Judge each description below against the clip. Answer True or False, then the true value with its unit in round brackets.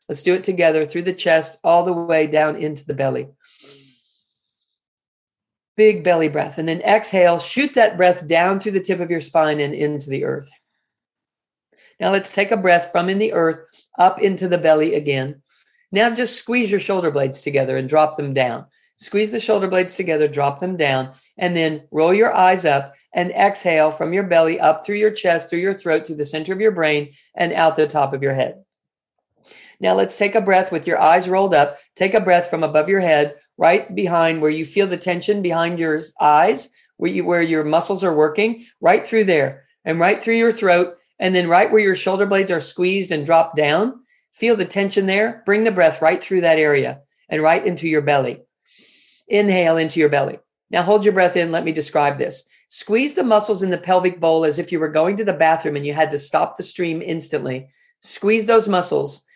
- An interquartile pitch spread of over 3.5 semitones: True (4.2 semitones)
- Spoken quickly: True (210 wpm)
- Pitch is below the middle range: False (170 Hz)